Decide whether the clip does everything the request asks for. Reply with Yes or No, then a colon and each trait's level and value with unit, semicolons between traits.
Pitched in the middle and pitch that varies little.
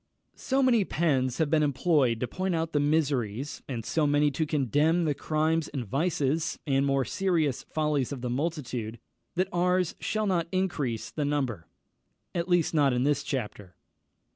No: medium, 150 Hz; average, 3.9 semitones